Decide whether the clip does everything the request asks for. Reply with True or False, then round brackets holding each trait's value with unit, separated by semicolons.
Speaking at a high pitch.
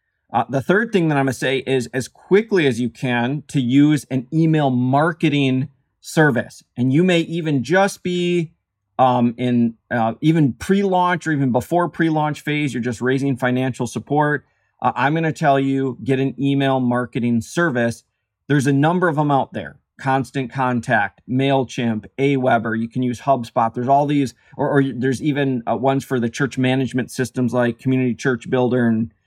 False (135 Hz)